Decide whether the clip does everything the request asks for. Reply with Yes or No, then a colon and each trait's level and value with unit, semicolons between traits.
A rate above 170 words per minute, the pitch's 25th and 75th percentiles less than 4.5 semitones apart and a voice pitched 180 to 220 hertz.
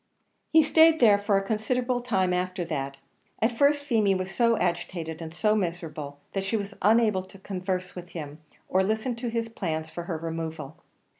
No: average, 180 wpm; average, 5.2 semitones; high, 190 Hz